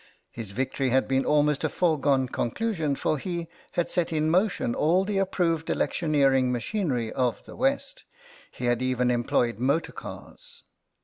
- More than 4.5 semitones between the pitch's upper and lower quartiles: Yes, wide, 5.5 semitones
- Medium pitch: Yes, medium, 150 Hz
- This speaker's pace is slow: No, average, 150 wpm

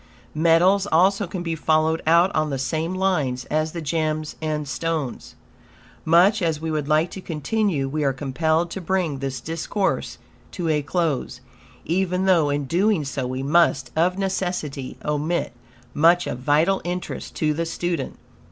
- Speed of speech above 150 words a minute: Yes, average, 160 wpm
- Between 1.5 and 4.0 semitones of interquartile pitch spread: Yes, average, 3.1 semitones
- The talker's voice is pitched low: No, medium, 160 Hz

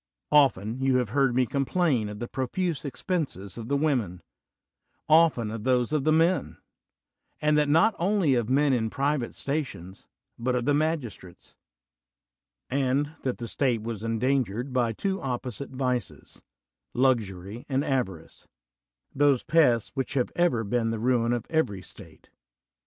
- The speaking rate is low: No, average, 150 wpm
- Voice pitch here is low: Yes, low, 130 Hz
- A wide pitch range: No, average, 4.2 semitones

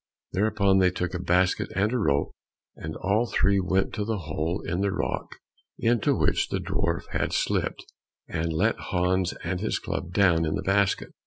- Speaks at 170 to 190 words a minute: Yes, average, 180 wpm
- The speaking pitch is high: No, very low, 95 Hz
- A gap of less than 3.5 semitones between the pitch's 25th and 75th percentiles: Yes, average, 2.8 semitones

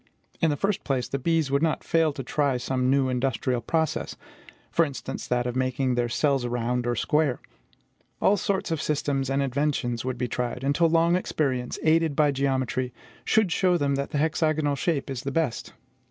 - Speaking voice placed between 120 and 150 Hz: Yes, medium, 140 Hz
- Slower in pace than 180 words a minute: No, average, 185 wpm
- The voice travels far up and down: No, average, 3.7 semitones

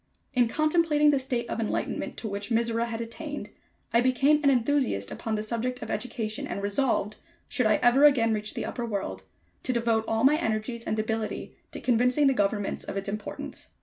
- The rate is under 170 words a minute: No, average, 190 wpm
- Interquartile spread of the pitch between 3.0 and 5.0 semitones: Yes, average, 3.3 semitones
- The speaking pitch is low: No, high, 235 Hz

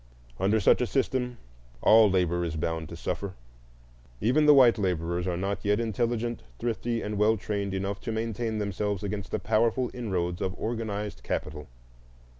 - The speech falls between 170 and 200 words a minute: No, average, 160 wpm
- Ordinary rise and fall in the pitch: Yes, average, 3.5 semitones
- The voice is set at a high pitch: No, low, 105 Hz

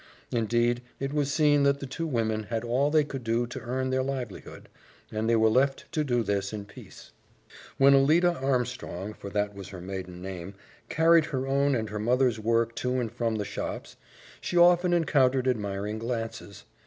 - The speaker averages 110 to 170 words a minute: No, average, 185 wpm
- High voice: No, low, 120 Hz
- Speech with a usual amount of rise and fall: Yes, average, 4.1 semitones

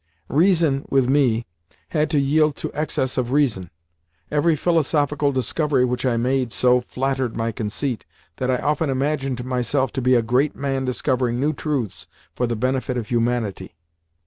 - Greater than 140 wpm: Yes, average, 160 wpm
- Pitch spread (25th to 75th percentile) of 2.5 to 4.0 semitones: Yes, average, 2.9 semitones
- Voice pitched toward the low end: Yes, low, 130 Hz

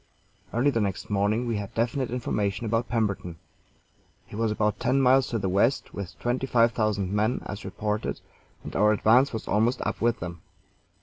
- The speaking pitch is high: No, low, 110 Hz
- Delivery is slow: No, average, 180 wpm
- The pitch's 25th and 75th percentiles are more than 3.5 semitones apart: No, average, 2.9 semitones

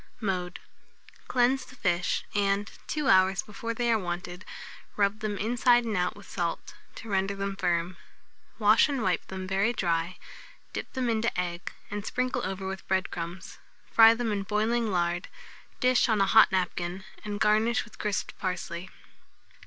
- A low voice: No, high, 200 Hz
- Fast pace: No, average, 160 wpm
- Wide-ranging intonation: No, average, 3.7 semitones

